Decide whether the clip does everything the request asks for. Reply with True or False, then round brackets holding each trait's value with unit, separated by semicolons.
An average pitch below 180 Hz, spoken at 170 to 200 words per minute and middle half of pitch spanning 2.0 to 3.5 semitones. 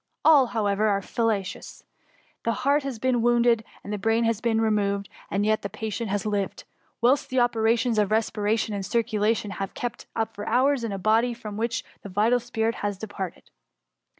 False (220 Hz; 185 wpm; 2.4 semitones)